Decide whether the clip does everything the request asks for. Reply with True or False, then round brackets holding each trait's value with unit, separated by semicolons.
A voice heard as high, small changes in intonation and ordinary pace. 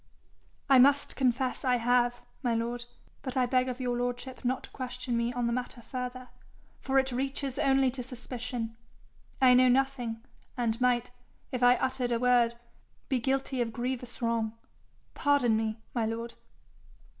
True (250 Hz; 1.5 semitones; 160 wpm)